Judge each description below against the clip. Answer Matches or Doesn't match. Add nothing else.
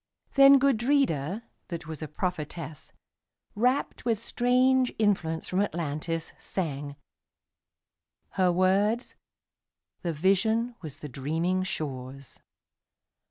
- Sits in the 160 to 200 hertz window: Matches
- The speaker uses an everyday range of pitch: Doesn't match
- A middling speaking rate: Doesn't match